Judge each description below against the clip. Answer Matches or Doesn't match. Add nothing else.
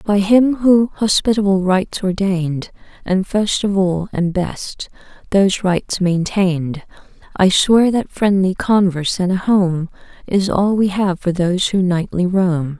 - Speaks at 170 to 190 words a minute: Doesn't match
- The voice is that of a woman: Matches